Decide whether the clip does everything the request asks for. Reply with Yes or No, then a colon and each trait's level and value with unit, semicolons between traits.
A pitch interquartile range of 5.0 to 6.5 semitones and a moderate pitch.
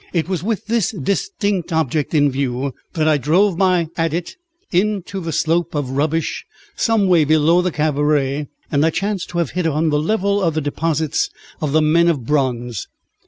No: average, 3.6 semitones; medium, 160 Hz